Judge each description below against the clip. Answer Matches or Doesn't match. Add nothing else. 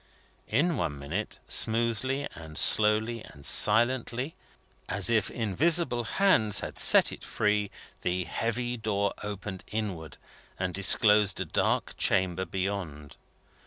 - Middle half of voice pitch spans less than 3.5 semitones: Doesn't match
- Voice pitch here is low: Matches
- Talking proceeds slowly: Matches